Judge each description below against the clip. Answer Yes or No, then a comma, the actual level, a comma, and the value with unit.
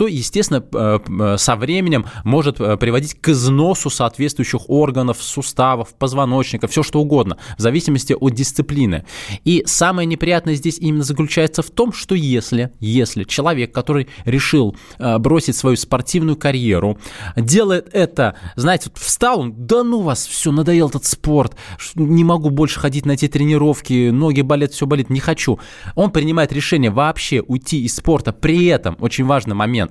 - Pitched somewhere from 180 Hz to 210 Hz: No, medium, 140 Hz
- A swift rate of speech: No, average, 150 wpm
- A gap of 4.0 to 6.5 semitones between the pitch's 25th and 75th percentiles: Yes, average, 4.6 semitones